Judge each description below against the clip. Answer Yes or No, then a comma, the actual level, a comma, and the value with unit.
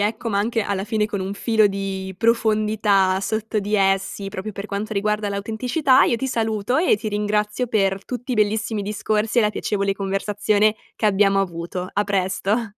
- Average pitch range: No, narrow, 1.8 semitones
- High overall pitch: Yes, high, 210 Hz